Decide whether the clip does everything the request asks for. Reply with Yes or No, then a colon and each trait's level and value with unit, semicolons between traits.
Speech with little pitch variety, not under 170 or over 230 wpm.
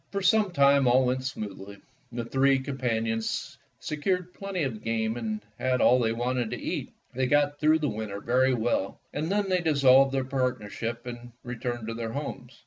No: average, 3.8 semitones; average, 180 wpm